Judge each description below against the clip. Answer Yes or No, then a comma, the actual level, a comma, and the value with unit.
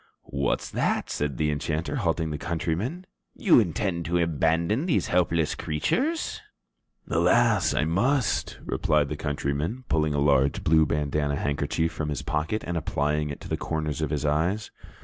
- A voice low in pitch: Yes, very low, 80 Hz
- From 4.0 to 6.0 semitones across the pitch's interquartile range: No, average, 2.9 semitones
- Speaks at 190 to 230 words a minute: No, average, 155 wpm